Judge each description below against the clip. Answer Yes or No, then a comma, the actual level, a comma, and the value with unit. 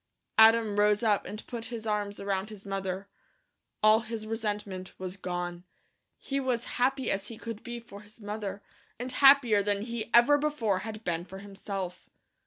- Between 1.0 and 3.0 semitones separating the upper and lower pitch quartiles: Yes, average, 2.7 semitones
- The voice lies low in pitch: No, high, 210 Hz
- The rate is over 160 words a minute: Yes, average, 170 wpm